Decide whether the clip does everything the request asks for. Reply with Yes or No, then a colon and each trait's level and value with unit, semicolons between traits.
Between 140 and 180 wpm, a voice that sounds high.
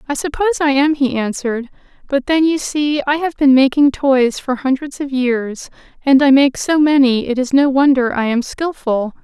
No: average, 200 wpm; very high, 270 Hz